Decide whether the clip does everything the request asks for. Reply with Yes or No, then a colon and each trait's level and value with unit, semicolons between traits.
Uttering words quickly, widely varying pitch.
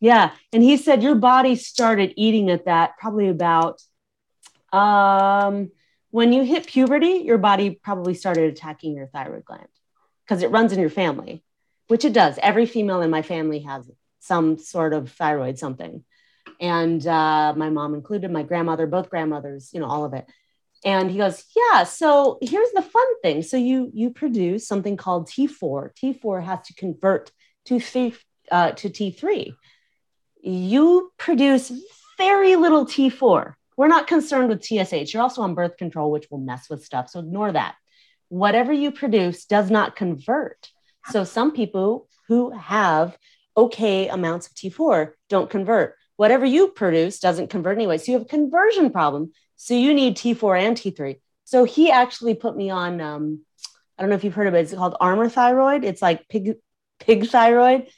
No: average, 170 wpm; wide, 6.7 semitones